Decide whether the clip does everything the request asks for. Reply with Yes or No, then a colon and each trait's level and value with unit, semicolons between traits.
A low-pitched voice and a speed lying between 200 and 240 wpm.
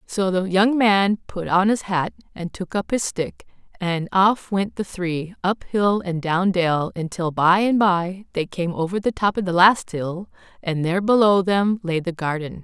No: medium, 185 Hz; fast, 205 wpm